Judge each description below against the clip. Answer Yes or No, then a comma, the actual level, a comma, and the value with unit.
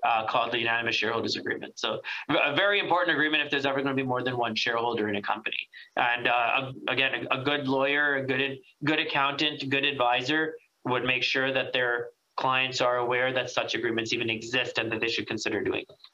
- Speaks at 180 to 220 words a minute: Yes, fast, 205 wpm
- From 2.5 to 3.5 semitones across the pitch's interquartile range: Yes, average, 2.8 semitones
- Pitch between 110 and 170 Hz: Yes, low, 130 Hz